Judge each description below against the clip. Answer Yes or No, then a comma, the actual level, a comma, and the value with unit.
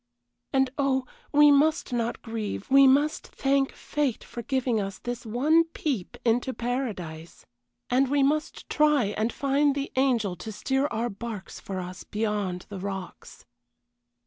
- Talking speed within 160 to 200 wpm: No, average, 145 wpm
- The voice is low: No, high, 245 Hz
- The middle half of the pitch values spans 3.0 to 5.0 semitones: Yes, average, 4.7 semitones